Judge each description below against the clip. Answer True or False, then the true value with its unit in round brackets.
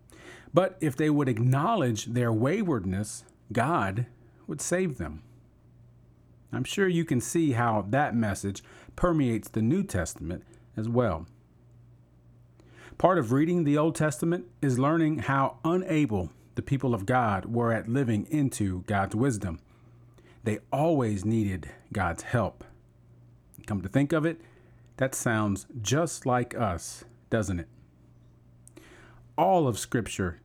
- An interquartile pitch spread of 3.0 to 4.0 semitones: False (4.6 semitones)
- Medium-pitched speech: False (120 Hz)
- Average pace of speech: False (130 wpm)